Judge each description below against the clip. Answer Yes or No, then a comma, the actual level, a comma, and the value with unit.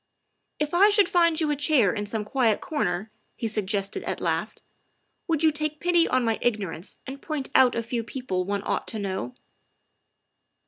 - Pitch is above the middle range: Yes, high, 245 Hz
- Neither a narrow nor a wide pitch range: No, wide, 6.8 semitones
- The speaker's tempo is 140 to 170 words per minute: No, average, 195 wpm